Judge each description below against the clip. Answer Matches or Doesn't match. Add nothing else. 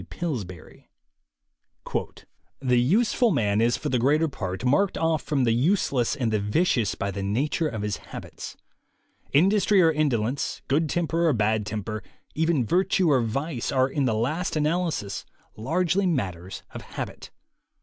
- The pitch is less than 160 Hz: Matches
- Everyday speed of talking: Matches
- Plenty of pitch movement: Matches